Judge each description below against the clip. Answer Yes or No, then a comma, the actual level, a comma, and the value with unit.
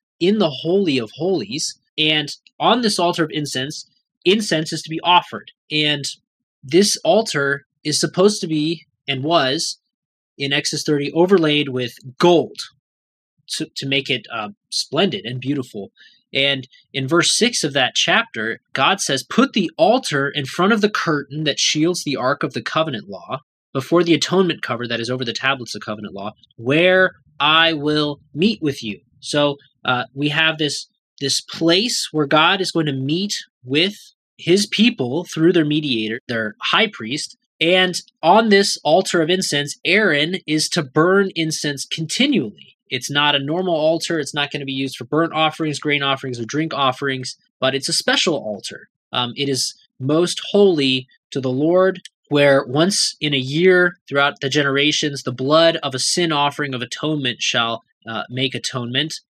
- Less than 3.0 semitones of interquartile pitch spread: No, average, 4.2 semitones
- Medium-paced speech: Yes, average, 170 wpm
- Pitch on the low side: No, medium, 150 Hz